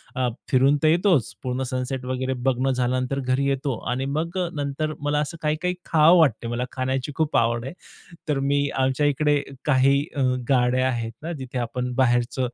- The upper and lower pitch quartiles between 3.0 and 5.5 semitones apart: No, narrow, 2.5 semitones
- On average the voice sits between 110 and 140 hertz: Yes, low, 135 Hz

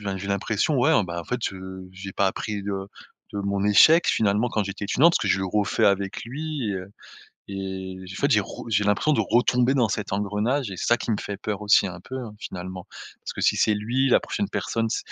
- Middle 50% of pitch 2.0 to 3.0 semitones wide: No, average, 3.6 semitones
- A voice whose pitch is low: Yes, low, 105 Hz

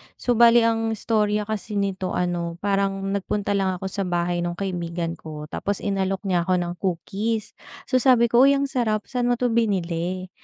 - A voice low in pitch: No, high, 195 Hz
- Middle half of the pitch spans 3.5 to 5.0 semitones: Yes, average, 4.0 semitones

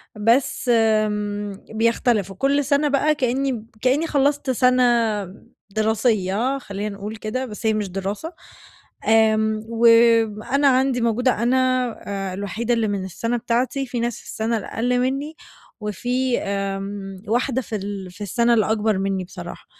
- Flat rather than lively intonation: No, average, 3.5 semitones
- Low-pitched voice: No, high, 225 Hz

